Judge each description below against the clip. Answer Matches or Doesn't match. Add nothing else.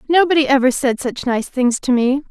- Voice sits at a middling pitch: Doesn't match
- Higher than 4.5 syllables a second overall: Matches